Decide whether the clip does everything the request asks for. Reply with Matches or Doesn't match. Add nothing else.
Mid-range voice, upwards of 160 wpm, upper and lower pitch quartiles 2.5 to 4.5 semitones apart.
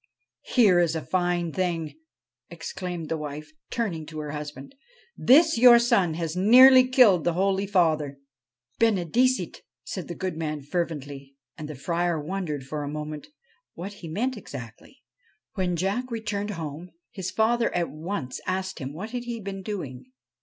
Doesn't match